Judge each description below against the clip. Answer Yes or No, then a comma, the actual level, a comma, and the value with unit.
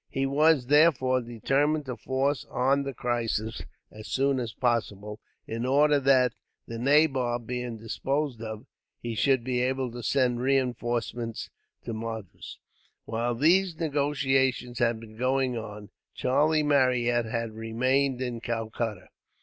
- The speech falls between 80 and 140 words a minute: Yes, slow, 135 wpm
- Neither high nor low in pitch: No, low, 125 Hz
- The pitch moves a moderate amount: Yes, average, 3.0 semitones